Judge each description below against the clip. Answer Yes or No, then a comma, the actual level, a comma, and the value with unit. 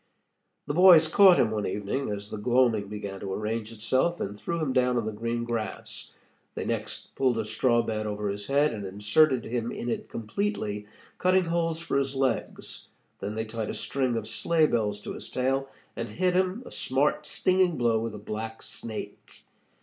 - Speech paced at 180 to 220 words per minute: Yes, average, 190 wpm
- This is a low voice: Yes, low, 120 Hz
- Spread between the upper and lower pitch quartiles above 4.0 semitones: Yes, wide, 5.4 semitones